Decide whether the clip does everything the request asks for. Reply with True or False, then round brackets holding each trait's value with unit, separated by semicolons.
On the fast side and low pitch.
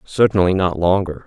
False (145 wpm; 90 Hz)